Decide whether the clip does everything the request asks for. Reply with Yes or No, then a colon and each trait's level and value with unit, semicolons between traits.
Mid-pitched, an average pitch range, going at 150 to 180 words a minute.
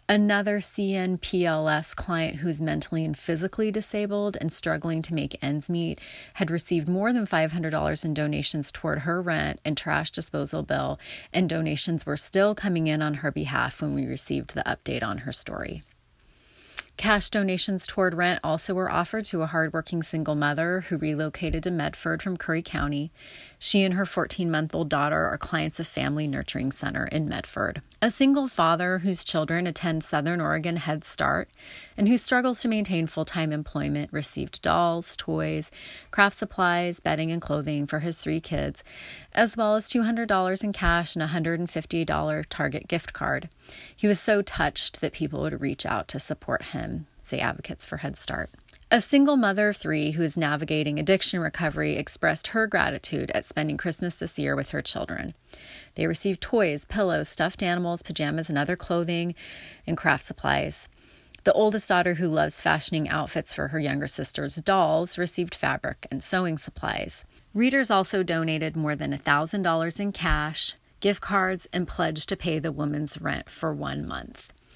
Yes: medium, 170 Hz; average, 3.8 semitones; average, 170 wpm